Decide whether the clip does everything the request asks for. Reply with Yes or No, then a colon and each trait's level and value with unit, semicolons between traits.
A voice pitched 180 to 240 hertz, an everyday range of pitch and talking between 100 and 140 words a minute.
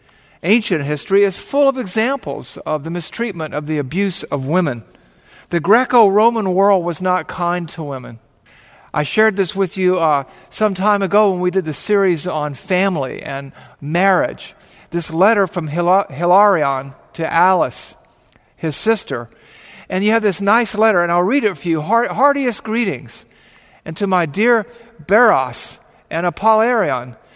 No: medium, 185 Hz; average, 4.9 semitones; average, 155 wpm